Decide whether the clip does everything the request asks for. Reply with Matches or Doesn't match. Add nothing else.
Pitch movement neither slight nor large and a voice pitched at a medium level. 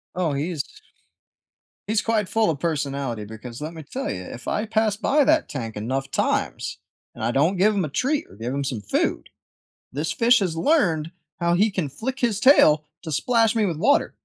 Doesn't match